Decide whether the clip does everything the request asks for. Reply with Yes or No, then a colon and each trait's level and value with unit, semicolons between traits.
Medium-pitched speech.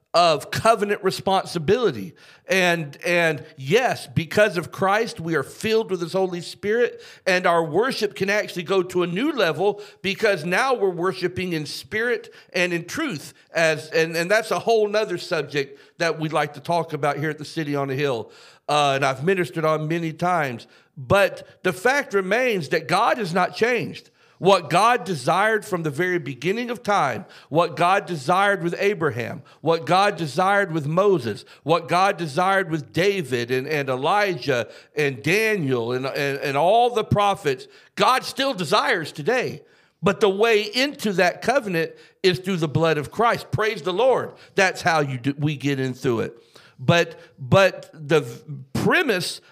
Yes: medium, 175 Hz